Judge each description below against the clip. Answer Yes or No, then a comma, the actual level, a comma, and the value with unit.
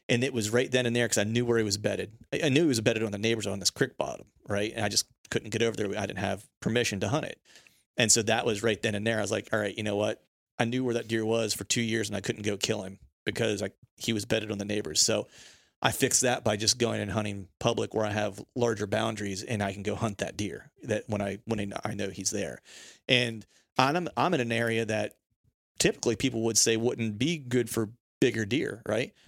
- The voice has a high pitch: No, low, 110 Hz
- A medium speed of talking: No, fast, 260 wpm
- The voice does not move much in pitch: Yes, narrow, 2.3 semitones